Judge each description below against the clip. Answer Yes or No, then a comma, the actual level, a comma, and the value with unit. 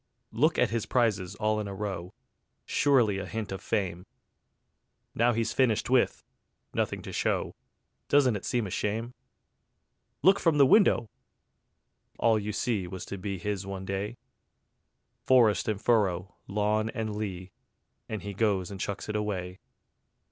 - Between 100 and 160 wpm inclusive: Yes, average, 150 wpm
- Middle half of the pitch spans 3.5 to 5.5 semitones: No, average, 3.0 semitones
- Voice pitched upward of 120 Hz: No, low, 105 Hz